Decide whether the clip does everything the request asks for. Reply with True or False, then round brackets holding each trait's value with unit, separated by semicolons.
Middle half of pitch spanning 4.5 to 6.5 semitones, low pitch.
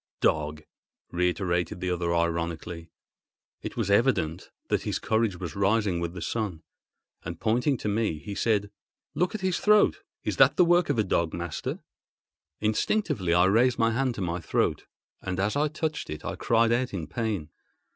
True (5.5 semitones; 100 Hz)